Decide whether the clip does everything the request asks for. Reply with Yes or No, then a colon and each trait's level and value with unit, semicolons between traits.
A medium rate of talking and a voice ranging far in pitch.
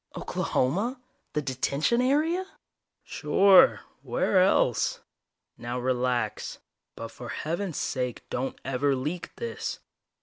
No: slow, 100 wpm; wide, 8.1 semitones